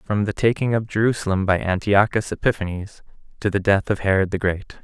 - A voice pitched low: Yes, low, 100 Hz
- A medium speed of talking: Yes, average, 185 wpm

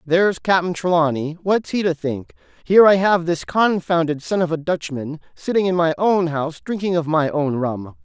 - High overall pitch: No, medium, 170 Hz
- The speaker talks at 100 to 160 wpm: No, average, 185 wpm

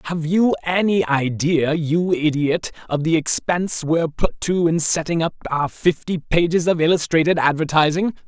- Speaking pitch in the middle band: Yes, medium, 165 Hz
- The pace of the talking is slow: No, average, 150 wpm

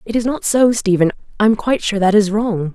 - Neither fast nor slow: No, fast, 240 wpm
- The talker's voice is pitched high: Yes, high, 210 Hz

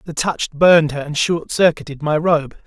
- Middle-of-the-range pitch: Yes, medium, 155 Hz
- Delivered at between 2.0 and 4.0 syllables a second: No, 4.9 syllables/s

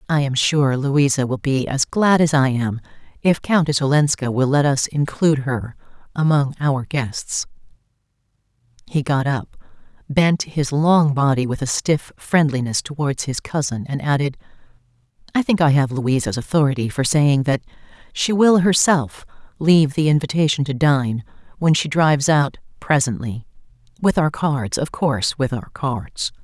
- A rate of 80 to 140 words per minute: No, average, 150 wpm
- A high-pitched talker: No, medium, 140 Hz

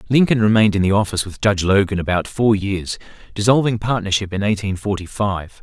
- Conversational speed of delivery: Yes, average, 180 wpm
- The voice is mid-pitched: No, low, 105 Hz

